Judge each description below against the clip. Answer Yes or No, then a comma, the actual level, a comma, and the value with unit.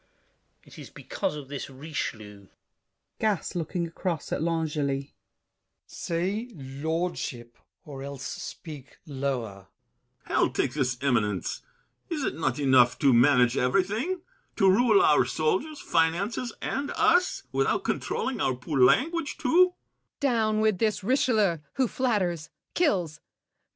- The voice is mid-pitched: Yes, medium, 155 Hz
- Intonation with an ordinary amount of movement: No, wide, 8.1 semitones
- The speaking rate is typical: No, slow, 100 wpm